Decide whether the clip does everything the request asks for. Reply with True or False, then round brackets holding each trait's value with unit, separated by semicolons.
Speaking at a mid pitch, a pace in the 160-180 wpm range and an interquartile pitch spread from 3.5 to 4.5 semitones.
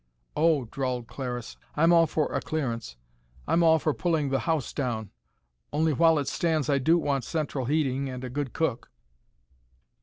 True (145 Hz; 170 wpm; 3.9 semitones)